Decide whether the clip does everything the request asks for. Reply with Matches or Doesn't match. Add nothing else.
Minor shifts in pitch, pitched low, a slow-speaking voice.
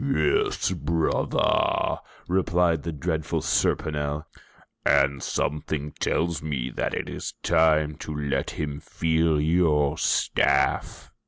Matches